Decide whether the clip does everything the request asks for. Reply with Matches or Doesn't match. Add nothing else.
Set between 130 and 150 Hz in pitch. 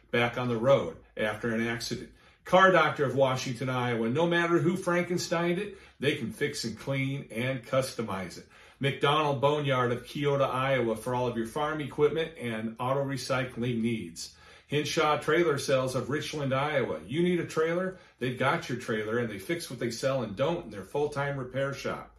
Matches